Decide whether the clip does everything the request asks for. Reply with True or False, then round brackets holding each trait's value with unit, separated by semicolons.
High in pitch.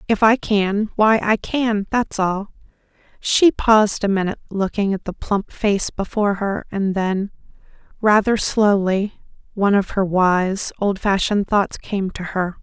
True (200 Hz)